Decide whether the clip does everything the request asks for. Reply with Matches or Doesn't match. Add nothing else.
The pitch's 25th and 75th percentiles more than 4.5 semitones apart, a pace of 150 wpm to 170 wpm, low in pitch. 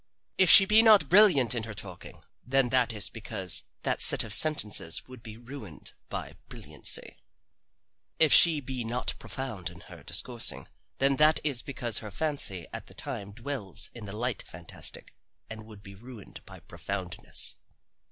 Matches